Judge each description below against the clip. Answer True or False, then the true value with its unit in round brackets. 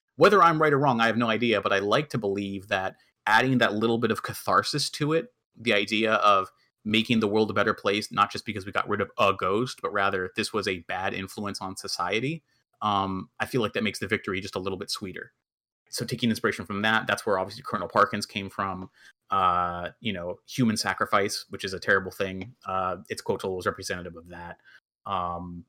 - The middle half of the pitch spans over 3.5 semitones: True (3.9 semitones)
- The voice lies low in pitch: True (110 Hz)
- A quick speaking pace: True (215 wpm)